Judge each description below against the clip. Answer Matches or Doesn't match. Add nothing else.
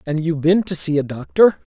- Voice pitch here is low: Doesn't match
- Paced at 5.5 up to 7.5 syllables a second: Matches